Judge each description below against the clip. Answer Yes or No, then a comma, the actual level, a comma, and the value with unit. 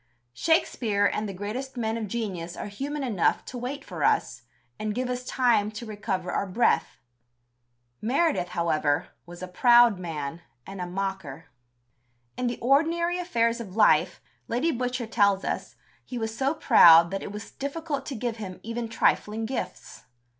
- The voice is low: No, high, 225 Hz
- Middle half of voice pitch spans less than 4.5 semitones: No, average, 4.8 semitones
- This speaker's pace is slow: No, average, 160 wpm